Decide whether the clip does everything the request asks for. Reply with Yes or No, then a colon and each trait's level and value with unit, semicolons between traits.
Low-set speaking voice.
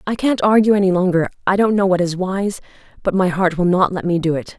No: medium, 185 Hz